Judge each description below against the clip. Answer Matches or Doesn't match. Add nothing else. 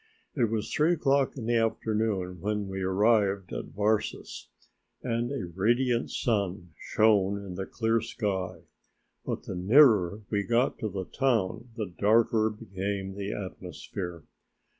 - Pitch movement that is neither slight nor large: Matches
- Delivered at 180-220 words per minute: Doesn't match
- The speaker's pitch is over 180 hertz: Doesn't match